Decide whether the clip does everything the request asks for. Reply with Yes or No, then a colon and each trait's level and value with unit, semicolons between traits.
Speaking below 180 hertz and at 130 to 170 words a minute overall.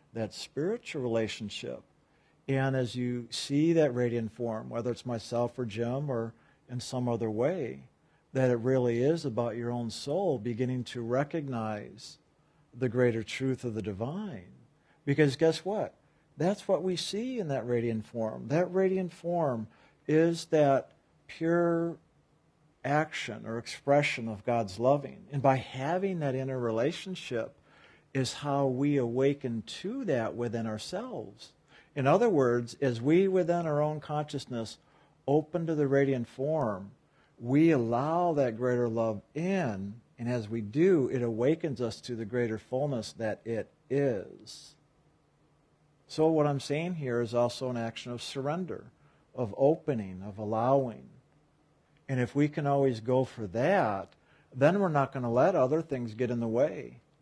Yes: low, 135 Hz; average, 150 wpm